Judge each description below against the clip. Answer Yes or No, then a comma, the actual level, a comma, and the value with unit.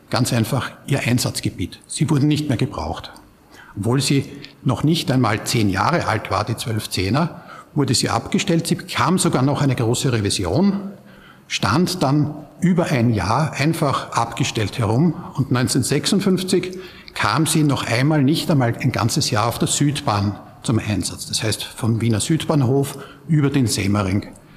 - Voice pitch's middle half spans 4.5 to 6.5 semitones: Yes, wide, 5.4 semitones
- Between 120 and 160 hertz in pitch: Yes, low, 135 Hz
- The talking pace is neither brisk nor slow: Yes, average, 155 wpm